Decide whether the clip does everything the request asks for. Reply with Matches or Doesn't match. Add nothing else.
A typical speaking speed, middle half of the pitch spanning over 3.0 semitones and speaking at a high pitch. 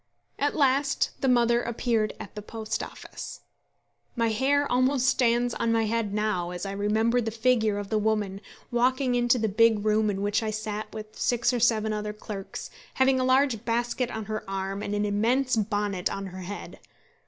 Doesn't match